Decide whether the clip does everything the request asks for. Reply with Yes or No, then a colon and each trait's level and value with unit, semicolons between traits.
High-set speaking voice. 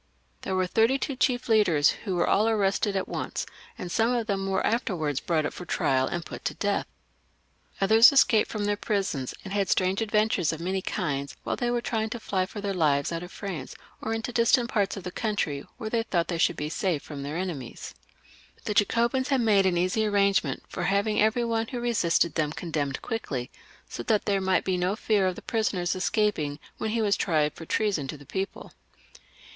Yes: high, 195 Hz